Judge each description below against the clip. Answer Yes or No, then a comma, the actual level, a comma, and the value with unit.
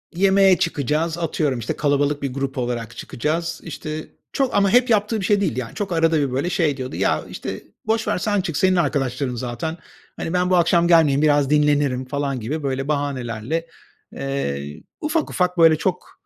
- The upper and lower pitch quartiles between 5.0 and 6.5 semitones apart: No, average, 4.6 semitones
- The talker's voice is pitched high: No, medium, 150 Hz